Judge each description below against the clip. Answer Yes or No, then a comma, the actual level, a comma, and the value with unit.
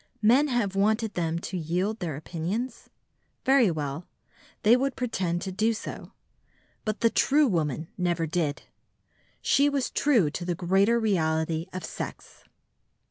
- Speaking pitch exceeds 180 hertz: Yes, high, 190 Hz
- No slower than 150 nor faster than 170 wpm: No, average, 140 wpm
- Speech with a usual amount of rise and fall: No, wide, 5.7 semitones